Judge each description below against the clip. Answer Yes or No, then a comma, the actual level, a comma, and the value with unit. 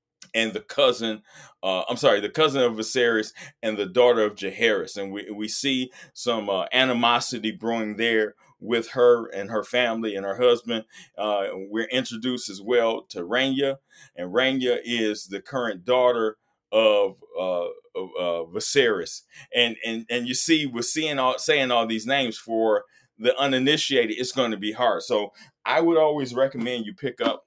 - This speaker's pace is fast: No, average, 170 wpm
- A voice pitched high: No, low, 120 Hz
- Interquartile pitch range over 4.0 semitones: No, average, 3.2 semitones